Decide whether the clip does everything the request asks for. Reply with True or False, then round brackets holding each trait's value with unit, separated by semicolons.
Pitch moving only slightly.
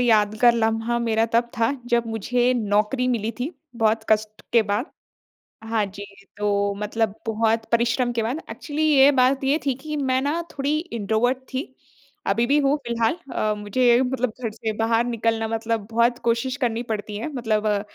True (2.3 semitones)